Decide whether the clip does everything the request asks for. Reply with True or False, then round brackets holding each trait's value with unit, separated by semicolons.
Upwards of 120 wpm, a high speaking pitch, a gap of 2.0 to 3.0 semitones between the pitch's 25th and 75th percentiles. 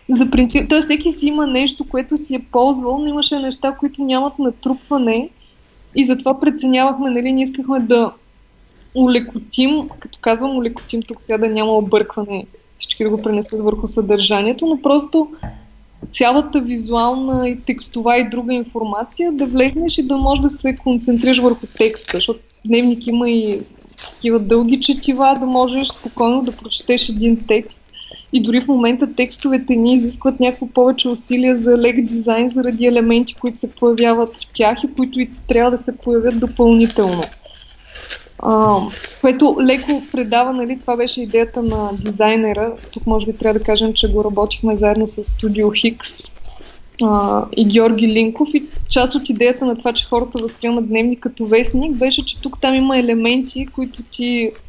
True (160 wpm; 245 Hz; 2.5 semitones)